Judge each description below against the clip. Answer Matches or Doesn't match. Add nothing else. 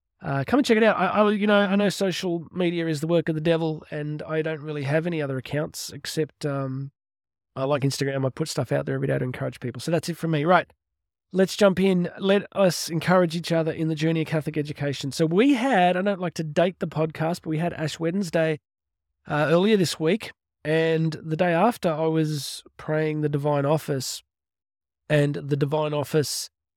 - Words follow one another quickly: Matches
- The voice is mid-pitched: Matches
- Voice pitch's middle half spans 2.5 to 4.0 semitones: Matches